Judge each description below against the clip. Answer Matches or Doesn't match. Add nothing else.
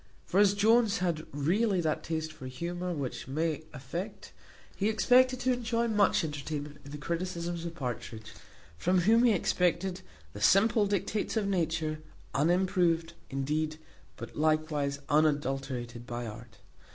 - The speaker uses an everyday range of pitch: Matches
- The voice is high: Doesn't match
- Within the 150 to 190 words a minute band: Doesn't match